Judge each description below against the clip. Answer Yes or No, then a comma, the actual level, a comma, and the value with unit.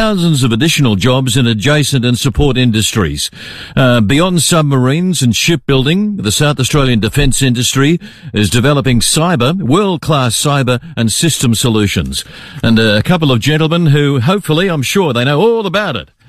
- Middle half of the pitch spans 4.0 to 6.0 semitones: Yes, average, 5.1 semitones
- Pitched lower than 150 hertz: Yes, medium, 140 Hz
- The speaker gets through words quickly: No, average, 150 wpm